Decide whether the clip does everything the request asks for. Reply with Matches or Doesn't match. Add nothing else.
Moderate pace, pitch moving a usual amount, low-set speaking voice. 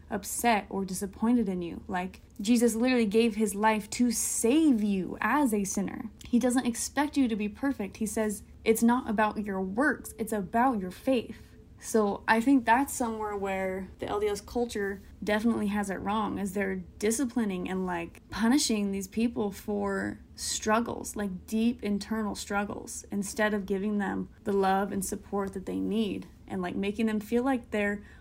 Doesn't match